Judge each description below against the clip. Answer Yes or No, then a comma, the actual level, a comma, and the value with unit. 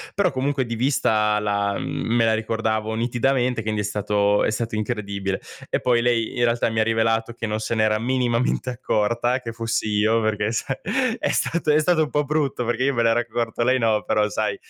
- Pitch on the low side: Yes, low, 115 Hz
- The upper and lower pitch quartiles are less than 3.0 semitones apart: Yes, narrow, 2.5 semitones